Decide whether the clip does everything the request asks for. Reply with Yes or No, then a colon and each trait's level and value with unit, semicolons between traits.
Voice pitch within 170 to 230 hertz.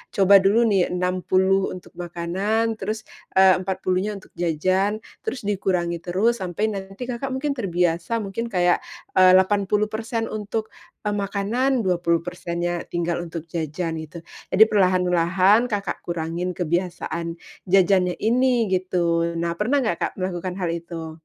Yes: medium, 185 Hz